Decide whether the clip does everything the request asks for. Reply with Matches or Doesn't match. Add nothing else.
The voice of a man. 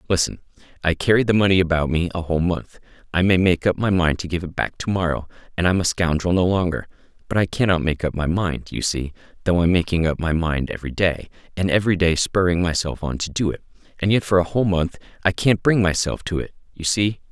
Matches